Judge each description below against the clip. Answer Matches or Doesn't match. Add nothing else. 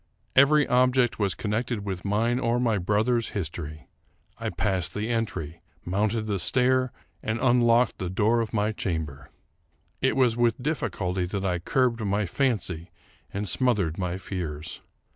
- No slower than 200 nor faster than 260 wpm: Doesn't match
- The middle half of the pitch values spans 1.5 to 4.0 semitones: Doesn't match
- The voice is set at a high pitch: Doesn't match